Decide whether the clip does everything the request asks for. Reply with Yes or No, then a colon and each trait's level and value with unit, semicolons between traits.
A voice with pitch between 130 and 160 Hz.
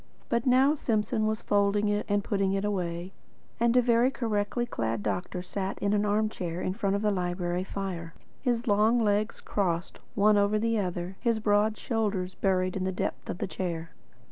No: high, 205 Hz